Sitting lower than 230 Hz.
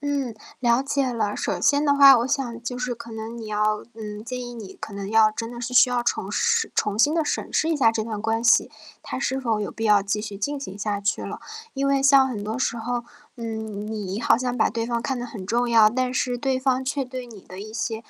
No: high, 235 Hz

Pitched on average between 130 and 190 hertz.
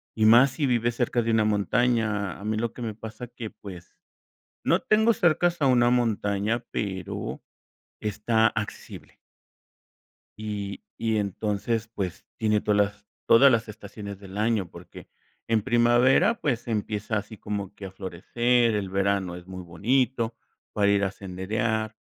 No: low, 110 Hz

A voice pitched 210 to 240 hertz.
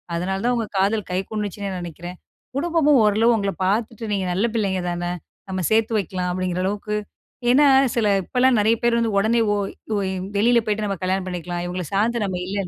No: high, 200 Hz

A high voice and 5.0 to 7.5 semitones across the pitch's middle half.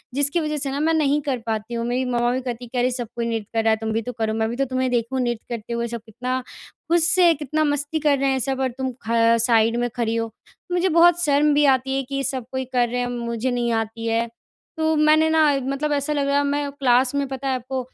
No: very high, 260 Hz; average, 3.3 semitones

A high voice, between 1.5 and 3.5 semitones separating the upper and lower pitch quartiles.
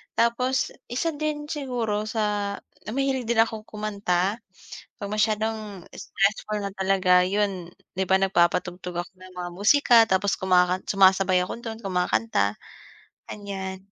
Yes: high, 200 Hz; average, 3.1 semitones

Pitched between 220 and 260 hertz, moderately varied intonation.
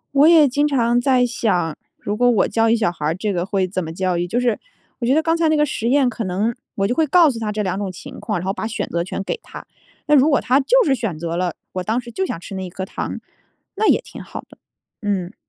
No: high, 225 Hz; wide, 6.1 semitones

